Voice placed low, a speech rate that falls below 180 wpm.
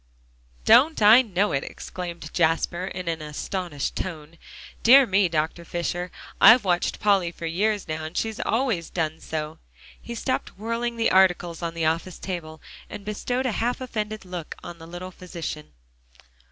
No: medium, 180 Hz; average, 160 wpm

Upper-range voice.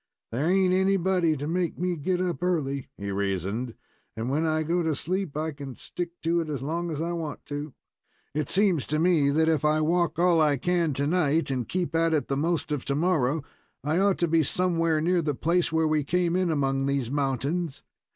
No: medium, 160 Hz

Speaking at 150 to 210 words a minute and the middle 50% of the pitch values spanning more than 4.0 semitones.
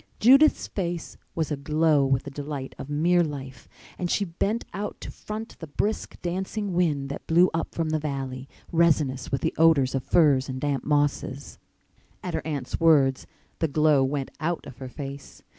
No: average, 175 wpm; average, 3.7 semitones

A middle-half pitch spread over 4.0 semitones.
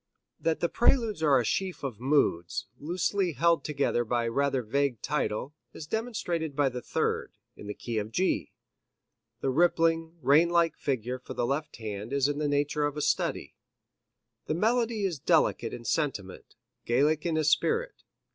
Yes: average, 5.0 semitones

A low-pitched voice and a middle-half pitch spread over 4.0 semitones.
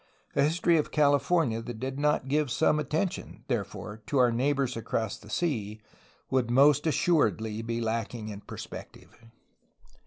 Yes: low, 130 Hz; average, 4.7 semitones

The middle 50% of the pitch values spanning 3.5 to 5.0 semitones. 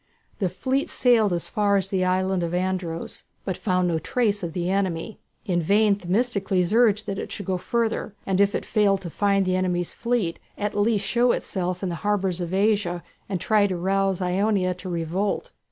No: narrow, 2.5 semitones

